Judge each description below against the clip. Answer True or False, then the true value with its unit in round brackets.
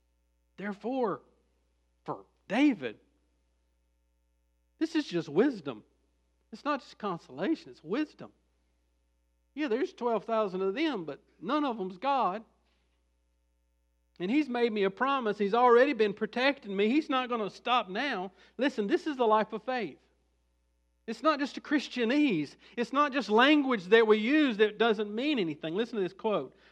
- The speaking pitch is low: False (215 Hz)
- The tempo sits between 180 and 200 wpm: False (150 wpm)